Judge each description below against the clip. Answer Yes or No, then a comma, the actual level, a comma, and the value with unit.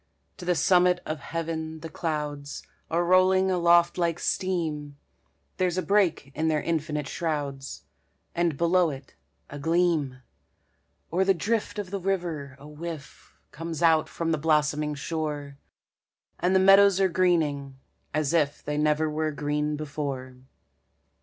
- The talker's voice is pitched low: No, medium, 160 Hz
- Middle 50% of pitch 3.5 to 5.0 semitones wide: No, average, 3.1 semitones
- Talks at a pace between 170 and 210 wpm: No, average, 140 wpm